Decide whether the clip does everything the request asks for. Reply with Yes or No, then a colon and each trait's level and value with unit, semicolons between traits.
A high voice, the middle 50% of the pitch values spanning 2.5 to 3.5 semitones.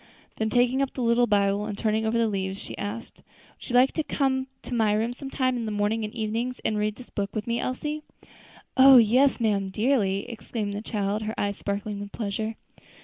Yes: high, 220 Hz; average, 3.1 semitones